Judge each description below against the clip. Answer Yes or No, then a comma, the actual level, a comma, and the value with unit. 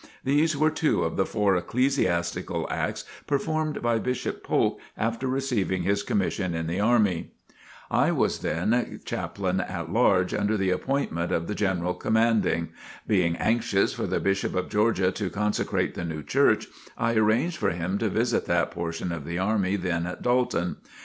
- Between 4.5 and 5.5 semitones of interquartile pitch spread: Yes, average, 4.9 semitones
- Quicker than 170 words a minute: No, average, 165 wpm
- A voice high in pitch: No, low, 100 Hz